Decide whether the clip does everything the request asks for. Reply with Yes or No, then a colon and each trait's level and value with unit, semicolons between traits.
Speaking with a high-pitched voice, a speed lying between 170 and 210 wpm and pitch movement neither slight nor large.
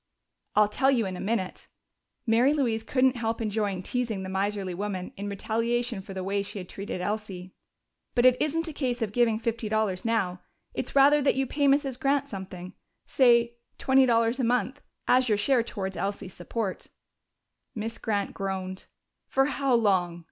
Yes: high, 225 Hz; average, 175 wpm; average, 4.3 semitones